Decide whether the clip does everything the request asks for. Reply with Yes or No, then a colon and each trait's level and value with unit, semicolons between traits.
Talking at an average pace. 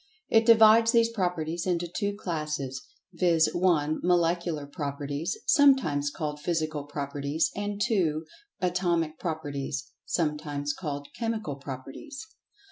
No: slow, 110 wpm